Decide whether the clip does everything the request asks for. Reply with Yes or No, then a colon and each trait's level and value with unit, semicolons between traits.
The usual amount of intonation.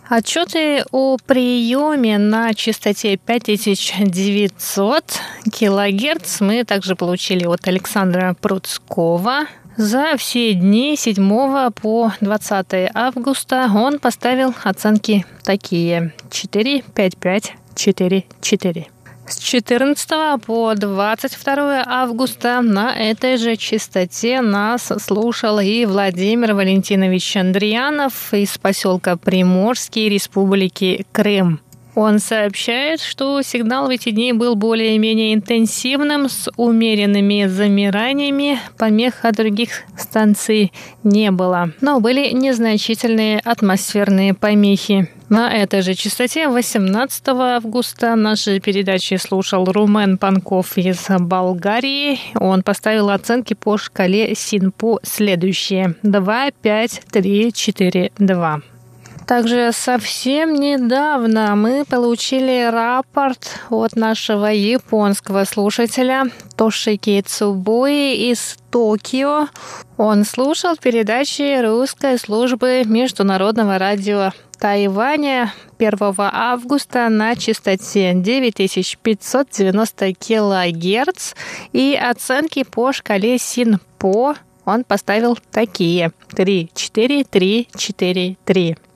Yes: average, 3.9 semitones